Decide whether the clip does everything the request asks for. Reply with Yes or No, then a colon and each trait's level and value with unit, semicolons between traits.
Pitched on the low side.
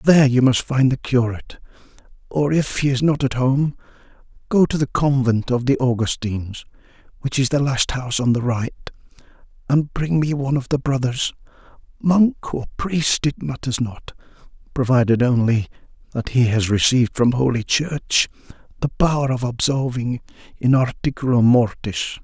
Yes: low, 130 Hz